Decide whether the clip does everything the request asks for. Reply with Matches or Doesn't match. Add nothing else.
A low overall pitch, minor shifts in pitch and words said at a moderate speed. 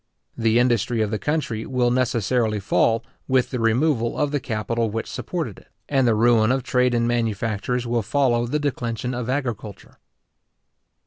Matches